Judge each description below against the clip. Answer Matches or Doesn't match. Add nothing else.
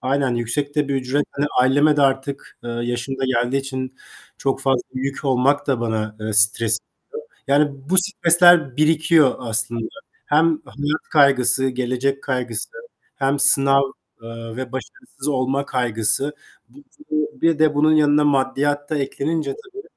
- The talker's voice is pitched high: Doesn't match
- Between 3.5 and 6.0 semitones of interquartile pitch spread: Doesn't match